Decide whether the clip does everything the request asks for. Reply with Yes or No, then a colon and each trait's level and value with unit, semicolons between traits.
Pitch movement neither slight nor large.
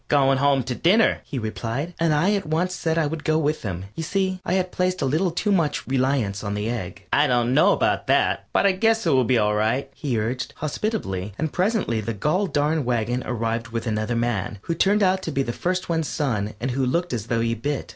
No: wide, 6.6 semitones